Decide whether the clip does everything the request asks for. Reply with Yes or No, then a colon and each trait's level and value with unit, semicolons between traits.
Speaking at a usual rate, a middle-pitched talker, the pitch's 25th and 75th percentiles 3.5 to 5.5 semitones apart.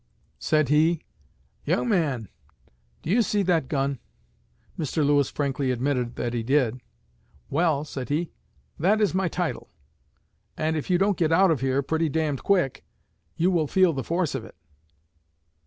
Yes: average, 160 wpm; medium, 155 Hz; average, 4.2 semitones